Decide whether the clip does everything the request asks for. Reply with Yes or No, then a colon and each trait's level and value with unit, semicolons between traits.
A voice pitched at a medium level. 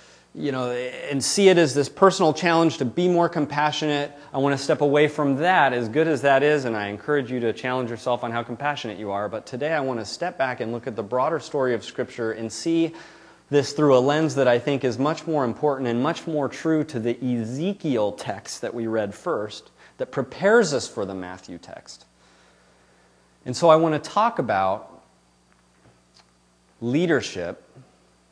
No: low, 130 Hz